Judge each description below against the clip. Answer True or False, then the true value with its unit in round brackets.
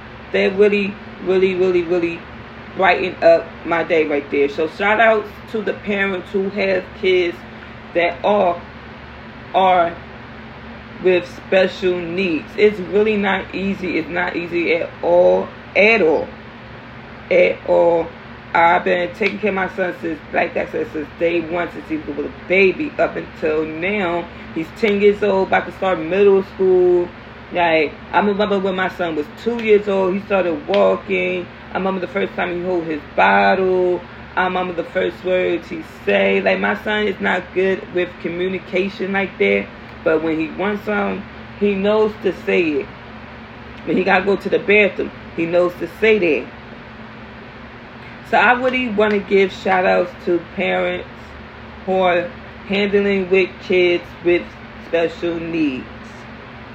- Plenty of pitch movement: False (3.8 semitones)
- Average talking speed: True (160 wpm)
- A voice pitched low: False (180 Hz)